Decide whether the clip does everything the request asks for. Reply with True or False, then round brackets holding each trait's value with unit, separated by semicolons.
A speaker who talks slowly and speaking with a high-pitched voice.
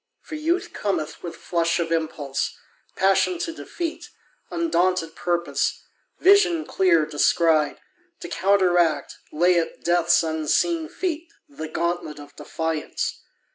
False (115 wpm; 175 Hz)